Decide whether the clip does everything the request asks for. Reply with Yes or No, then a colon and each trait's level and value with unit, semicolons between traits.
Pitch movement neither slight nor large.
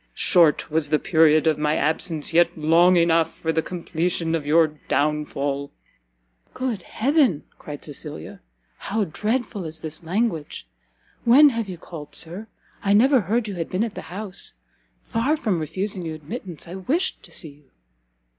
Yes: average, 5.0 semitones